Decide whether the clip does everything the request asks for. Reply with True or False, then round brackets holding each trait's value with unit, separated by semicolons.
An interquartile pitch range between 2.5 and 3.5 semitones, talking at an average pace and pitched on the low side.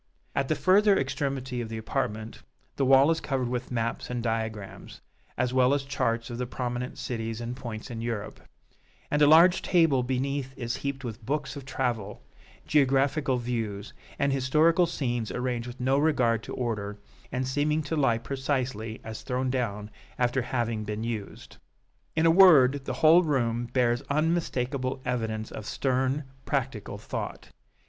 True (3.2 semitones; 160 wpm; 125 Hz)